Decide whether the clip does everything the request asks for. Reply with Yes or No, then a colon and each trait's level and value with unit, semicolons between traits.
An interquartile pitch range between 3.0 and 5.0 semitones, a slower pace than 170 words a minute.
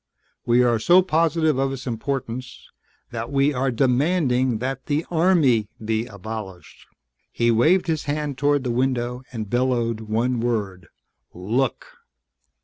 Yes: average, 3.8 semitones; slow, 135 wpm